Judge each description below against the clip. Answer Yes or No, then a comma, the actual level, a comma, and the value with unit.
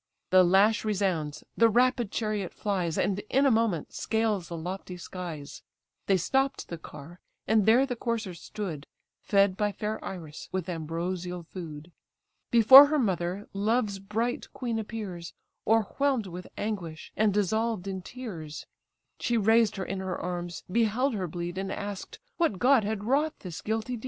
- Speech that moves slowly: No, average, 155 wpm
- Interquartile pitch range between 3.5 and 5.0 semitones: Yes, average, 4.1 semitones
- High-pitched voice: Yes, high, 200 Hz